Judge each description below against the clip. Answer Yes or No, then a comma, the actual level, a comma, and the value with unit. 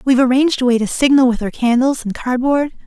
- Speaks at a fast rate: Yes, fast, 250 wpm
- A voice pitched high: Yes, very high, 255 Hz